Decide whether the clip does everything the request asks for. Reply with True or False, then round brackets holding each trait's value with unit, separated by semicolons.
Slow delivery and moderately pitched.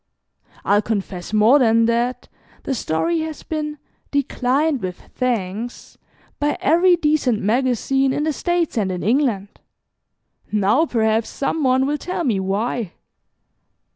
False (130 wpm; 250 Hz)